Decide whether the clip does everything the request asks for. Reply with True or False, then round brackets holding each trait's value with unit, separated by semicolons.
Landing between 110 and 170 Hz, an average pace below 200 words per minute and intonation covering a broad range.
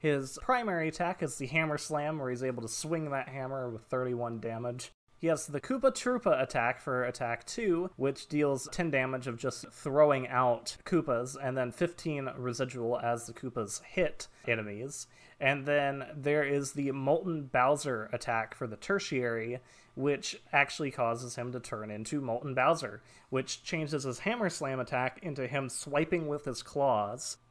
False (135 Hz; 165 wpm; 3.5 semitones)